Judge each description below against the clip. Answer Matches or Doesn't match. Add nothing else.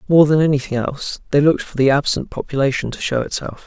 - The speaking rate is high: Matches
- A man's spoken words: Matches